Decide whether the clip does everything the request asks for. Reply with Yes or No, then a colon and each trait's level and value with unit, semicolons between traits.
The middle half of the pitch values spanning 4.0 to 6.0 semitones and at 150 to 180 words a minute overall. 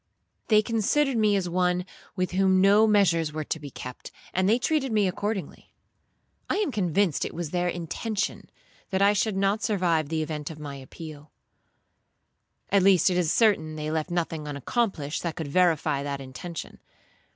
Yes: average, 4.6 semitones; average, 170 wpm